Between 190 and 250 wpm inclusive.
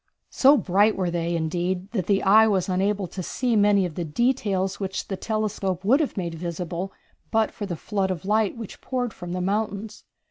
Yes: average, 200 wpm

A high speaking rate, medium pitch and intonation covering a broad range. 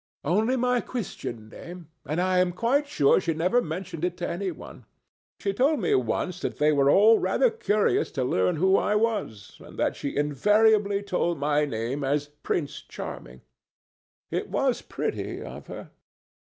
No: average, 170 wpm; medium, 180 Hz; wide, 6.4 semitones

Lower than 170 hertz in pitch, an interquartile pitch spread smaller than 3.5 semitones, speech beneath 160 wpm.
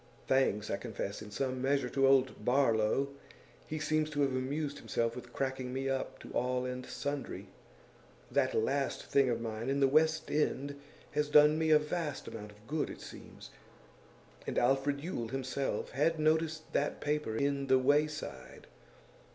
No: low, 135 Hz; average, 2.9 semitones; average, 165 wpm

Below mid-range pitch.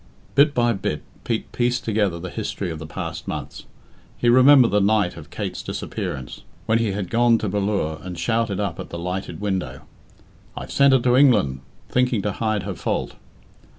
Yes: low, 105 Hz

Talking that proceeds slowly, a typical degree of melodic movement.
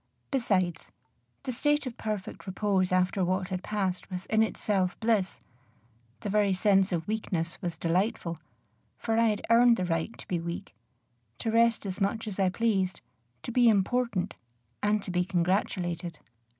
No: average, 160 wpm; average, 3.3 semitones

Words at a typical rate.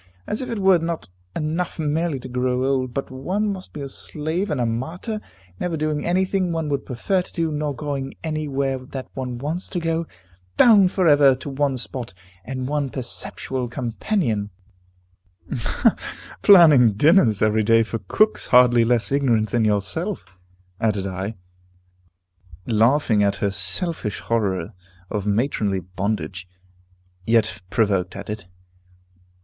Yes: average, 145 wpm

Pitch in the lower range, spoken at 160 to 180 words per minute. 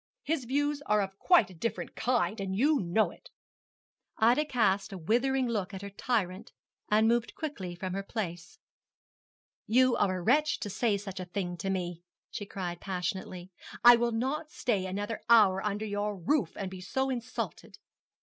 No: high, 210 Hz; average, 175 wpm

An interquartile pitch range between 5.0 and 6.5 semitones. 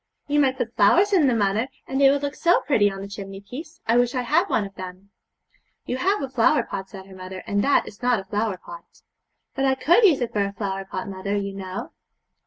Yes: wide, 5.6 semitones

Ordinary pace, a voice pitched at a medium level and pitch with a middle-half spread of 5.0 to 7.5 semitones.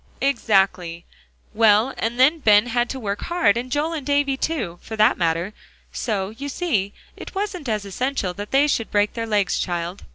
No: average, 185 wpm; high, 225 Hz; wide, 5.4 semitones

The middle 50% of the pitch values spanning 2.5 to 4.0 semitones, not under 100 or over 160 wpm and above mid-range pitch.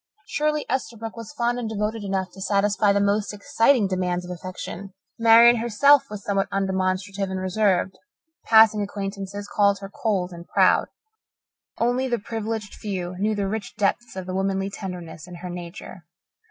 Yes: average, 2.8 semitones; average, 155 wpm; high, 200 Hz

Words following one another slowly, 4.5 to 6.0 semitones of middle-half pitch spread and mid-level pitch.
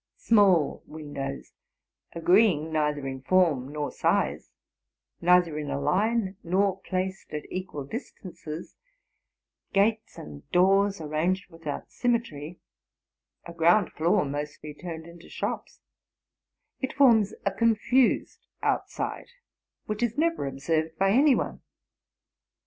Yes: slow, 110 wpm; average, 5.2 semitones; medium, 175 Hz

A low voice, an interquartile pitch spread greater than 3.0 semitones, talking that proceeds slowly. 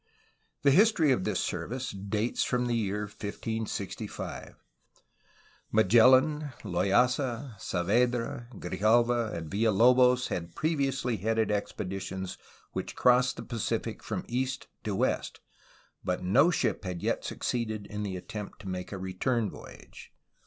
Yes: low, 115 Hz; average, 4.2 semitones; slow, 130 wpm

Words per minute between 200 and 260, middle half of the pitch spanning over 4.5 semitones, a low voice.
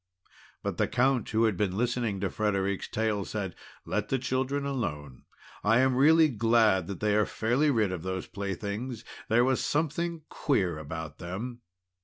No: average, 165 wpm; average, 4.9 semitones; low, 110 Hz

